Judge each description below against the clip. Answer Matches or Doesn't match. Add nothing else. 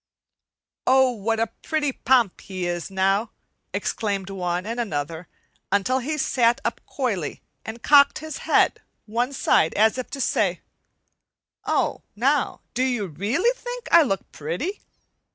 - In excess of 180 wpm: Doesn't match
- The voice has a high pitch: Matches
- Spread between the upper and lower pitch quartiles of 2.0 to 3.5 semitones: Doesn't match